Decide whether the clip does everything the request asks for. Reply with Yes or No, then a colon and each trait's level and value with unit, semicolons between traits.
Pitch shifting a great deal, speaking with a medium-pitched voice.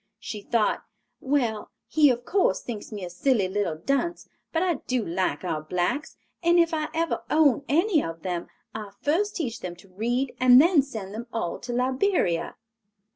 No: wide, 7.7 semitones; high, 245 Hz